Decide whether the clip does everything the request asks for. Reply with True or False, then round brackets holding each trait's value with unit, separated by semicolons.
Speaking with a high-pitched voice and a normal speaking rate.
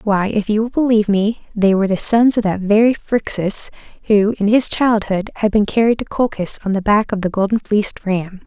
False (210 Hz; 220 wpm)